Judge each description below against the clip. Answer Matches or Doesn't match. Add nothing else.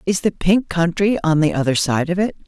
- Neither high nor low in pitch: Matches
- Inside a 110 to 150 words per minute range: Doesn't match